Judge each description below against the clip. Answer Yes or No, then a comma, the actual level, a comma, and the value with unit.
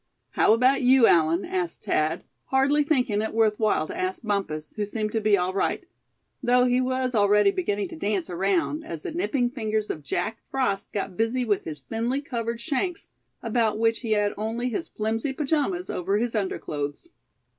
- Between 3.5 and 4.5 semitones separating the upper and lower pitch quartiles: Yes, average, 4.2 semitones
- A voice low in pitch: No, high, 220 Hz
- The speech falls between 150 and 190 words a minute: Yes, average, 180 wpm